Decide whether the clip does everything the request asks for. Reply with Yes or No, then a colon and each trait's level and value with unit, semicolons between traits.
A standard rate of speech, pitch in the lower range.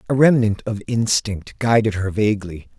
Yes: average, 150 wpm; low, 110 Hz